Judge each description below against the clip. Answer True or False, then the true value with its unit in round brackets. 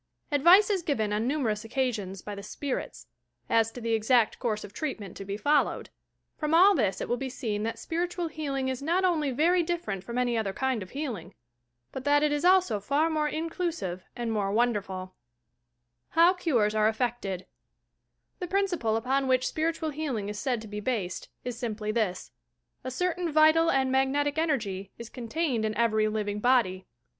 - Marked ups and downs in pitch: True (6.3 semitones)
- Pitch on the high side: True (250 Hz)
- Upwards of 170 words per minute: True (180 wpm)